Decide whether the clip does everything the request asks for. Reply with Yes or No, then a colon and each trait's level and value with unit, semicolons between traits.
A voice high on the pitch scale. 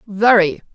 Yes: high, 205 Hz